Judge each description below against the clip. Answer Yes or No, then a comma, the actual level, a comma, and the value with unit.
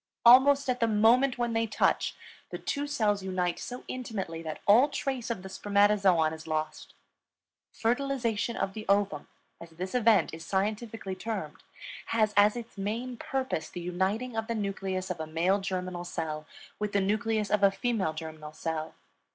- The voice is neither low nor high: No, high, 205 Hz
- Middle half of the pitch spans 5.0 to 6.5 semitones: No, average, 4.3 semitones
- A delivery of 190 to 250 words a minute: No, average, 165 wpm